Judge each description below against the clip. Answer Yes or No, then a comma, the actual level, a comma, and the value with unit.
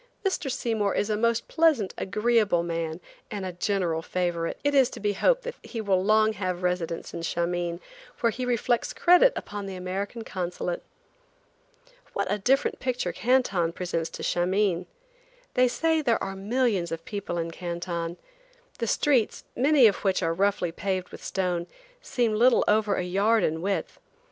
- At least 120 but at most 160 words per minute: No, average, 170 wpm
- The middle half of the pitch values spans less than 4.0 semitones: No, average, 4.9 semitones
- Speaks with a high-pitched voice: Yes, high, 200 Hz